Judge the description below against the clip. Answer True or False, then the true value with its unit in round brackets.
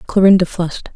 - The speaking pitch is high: False (180 Hz)